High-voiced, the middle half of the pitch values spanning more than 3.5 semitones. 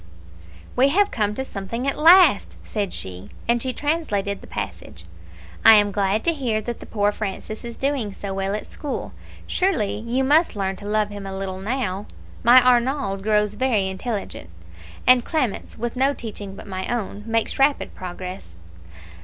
Yes: high, 215 Hz; average, 4.7 semitones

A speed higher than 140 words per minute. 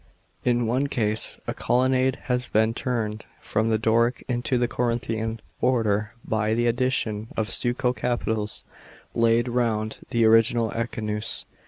No: slow, 135 wpm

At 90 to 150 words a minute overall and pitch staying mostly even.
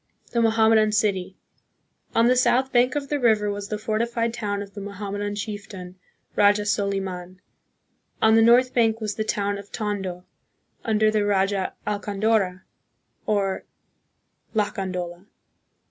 Yes: slow, 135 wpm; narrow, 2.0 semitones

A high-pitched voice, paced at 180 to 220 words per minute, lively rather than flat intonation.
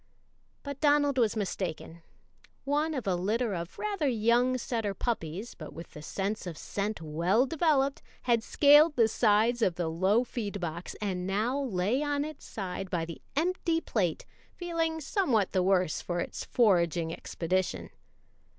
No: high, 220 Hz; average, 155 wpm; wide, 7.3 semitones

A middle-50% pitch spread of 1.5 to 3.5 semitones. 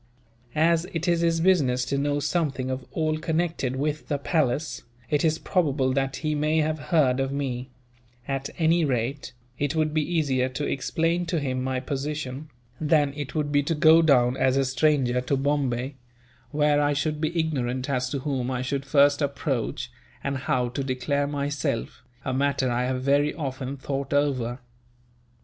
Yes: average, 2.8 semitones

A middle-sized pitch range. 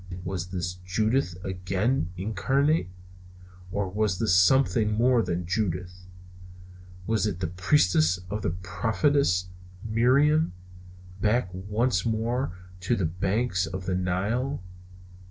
Yes: average, 4.4 semitones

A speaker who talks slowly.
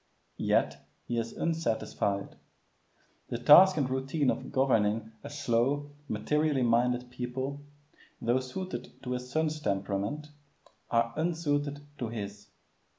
Yes: slow, 115 wpm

